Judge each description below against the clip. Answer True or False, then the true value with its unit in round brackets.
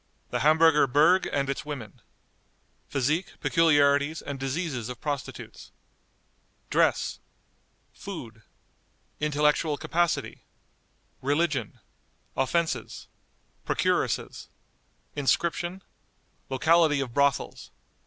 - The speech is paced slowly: True (75 wpm)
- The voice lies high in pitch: False (145 Hz)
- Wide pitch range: False (3.3 semitones)